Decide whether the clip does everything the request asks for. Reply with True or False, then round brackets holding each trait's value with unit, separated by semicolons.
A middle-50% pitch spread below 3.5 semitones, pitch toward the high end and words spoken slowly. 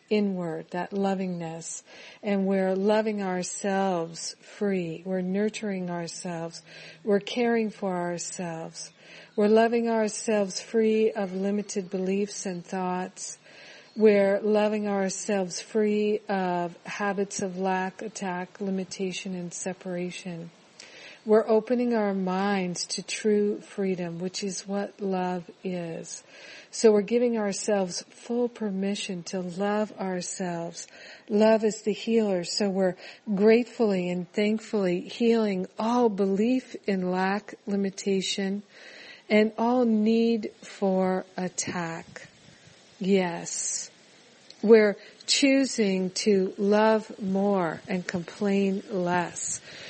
True (2.7 semitones; 200 Hz; 105 wpm)